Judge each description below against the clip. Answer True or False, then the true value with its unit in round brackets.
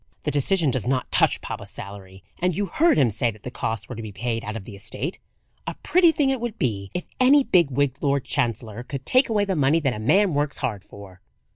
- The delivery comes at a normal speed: False (240 wpm)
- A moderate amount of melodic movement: False (8.5 semitones)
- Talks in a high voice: False (135 Hz)